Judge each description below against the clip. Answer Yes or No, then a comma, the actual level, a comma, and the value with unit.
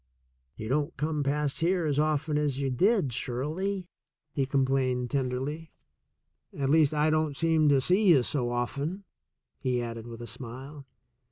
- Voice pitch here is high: No, medium, 140 Hz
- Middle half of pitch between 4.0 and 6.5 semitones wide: No, average, 3.5 semitones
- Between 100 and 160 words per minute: Yes, average, 155 wpm